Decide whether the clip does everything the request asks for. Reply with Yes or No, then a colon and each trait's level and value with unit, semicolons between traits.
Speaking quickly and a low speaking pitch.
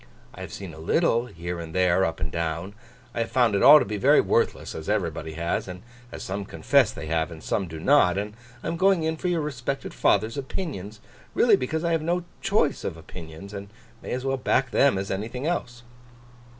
Yes: fast, 215 wpm; low, 105 Hz